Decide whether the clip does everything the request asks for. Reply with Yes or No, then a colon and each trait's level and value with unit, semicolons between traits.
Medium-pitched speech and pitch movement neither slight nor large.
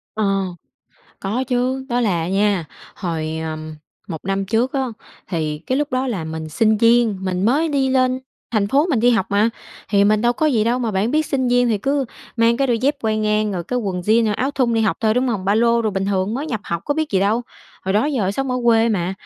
No: high, 225 Hz; average, 4.4 semitones